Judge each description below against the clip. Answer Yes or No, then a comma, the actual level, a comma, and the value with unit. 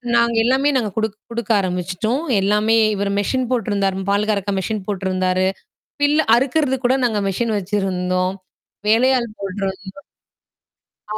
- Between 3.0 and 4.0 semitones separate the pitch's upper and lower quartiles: Yes, average, 3.7 semitones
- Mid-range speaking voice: No, high, 210 Hz